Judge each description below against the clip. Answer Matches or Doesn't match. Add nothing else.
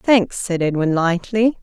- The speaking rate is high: Doesn't match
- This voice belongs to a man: Doesn't match